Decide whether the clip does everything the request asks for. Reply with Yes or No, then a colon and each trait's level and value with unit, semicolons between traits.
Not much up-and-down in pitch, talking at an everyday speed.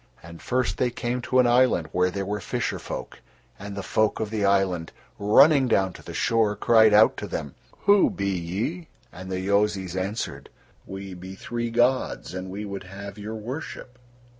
No: average, 4.0 semitones; average, 180 wpm